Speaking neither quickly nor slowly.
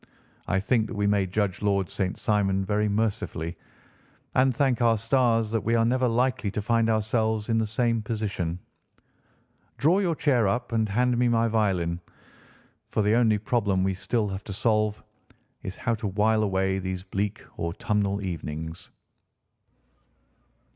Yes: average, 155 wpm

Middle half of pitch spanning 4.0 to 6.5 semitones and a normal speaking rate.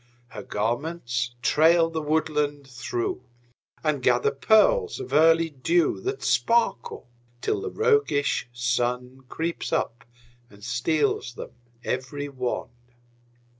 No: average, 5.3 semitones; slow, 110 wpm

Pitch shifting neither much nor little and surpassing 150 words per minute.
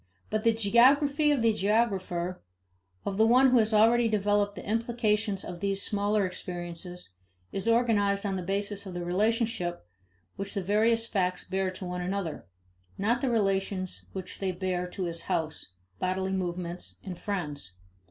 Yes: average, 3.5 semitones; average, 160 wpm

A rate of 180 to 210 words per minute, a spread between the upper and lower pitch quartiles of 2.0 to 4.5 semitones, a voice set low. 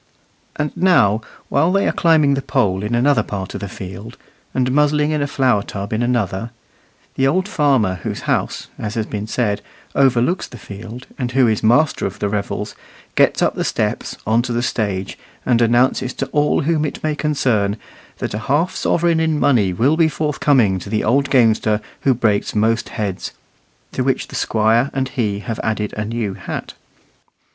No: average, 185 wpm; average, 5.1 semitones; low, 120 Hz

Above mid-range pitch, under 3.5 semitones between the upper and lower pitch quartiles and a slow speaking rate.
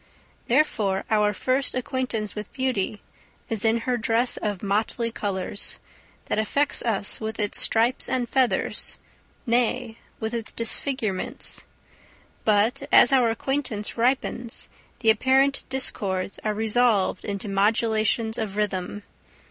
Yes: high, 225 Hz; average, 3.1 semitones; slow, 120 wpm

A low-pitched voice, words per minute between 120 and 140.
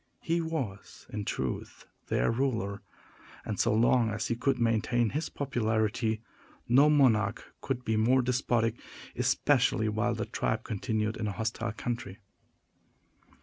Yes: low, 115 Hz; slow, 135 wpm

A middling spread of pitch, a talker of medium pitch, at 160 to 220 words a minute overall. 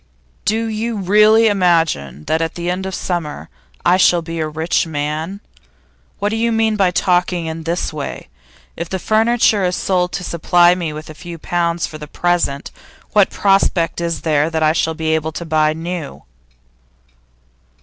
Yes: average, 3.1 semitones; medium, 175 Hz; average, 180 wpm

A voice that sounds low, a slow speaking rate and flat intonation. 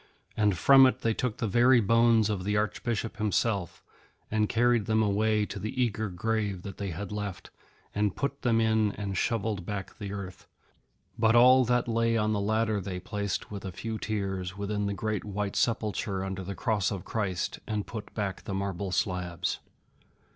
No: low, 105 Hz; average, 185 wpm; narrow, 2.3 semitones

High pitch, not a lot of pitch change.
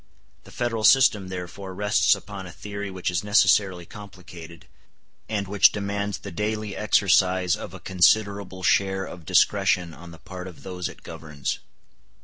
No: very low, 95 Hz; narrow, 2.3 semitones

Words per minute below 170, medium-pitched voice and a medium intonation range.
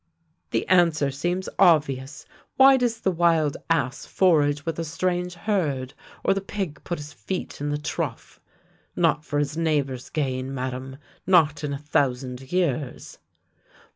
Yes: average, 155 wpm; medium, 150 Hz; average, 4.1 semitones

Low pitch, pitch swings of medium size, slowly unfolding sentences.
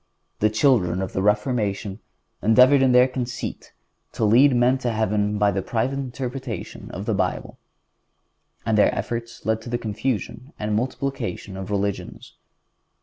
No: low, 115 Hz; average, 3.5 semitones; average, 150 wpm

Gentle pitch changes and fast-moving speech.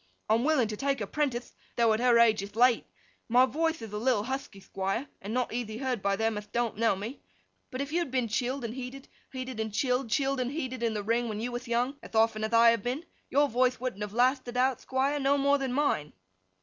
No: average, 3.1 semitones; fast, 240 wpm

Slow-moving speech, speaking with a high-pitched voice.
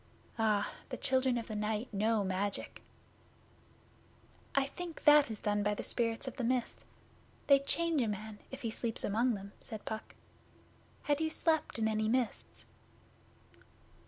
No: average, 155 wpm; high, 230 Hz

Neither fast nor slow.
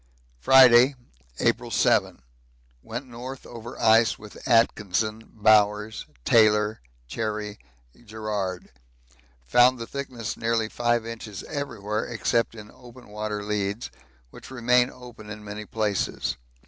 No: slow, 110 wpm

